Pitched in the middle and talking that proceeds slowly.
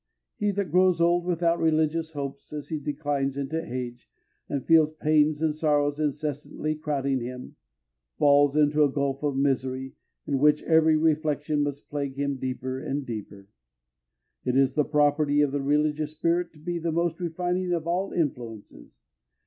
No: medium, 150 Hz; average, 160 wpm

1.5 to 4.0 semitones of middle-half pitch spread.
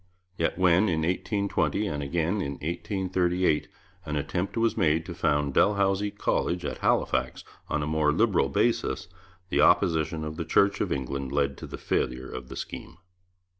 No: average, 4.4 semitones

